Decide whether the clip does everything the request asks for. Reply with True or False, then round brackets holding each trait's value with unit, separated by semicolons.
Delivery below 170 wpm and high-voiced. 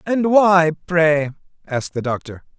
False (140 wpm; 160 Hz)